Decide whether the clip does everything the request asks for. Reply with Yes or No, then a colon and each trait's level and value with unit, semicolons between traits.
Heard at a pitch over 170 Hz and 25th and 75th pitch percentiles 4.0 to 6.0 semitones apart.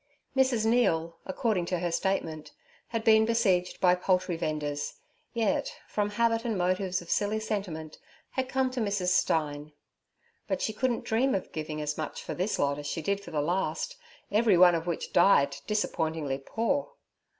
Yes: medium, 185 Hz; wide, 5.5 semitones